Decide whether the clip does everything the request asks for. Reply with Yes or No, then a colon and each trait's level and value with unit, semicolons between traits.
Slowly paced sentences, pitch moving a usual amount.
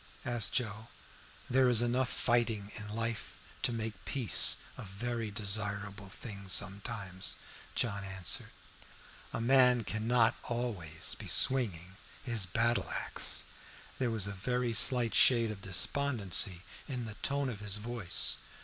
Yes: slow, 130 wpm; average, 3.3 semitones